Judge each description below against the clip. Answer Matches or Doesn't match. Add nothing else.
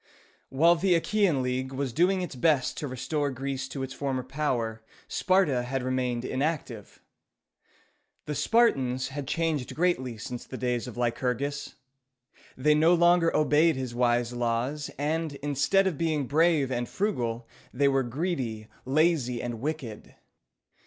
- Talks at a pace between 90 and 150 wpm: Matches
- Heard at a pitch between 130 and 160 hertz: Matches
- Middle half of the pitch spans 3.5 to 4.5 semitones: Matches